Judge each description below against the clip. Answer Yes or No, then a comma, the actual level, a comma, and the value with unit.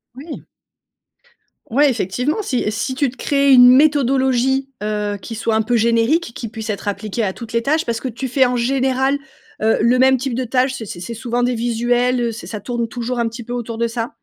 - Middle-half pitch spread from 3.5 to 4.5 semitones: No, narrow, 2.5 semitones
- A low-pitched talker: No, high, 245 Hz